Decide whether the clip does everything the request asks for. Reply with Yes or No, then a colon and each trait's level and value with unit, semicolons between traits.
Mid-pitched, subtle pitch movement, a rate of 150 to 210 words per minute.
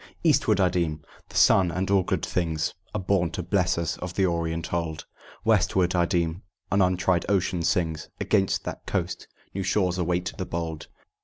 No: very low, 90 Hz; narrow, 2.2 semitones; average, 175 wpm